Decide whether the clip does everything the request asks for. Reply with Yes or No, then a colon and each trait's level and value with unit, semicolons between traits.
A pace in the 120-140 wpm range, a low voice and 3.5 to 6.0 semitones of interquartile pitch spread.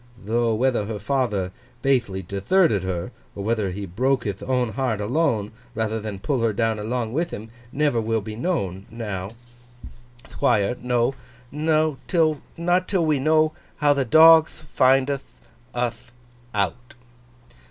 Yes: slow, 135 wpm; low, 120 Hz; average, 5.1 semitones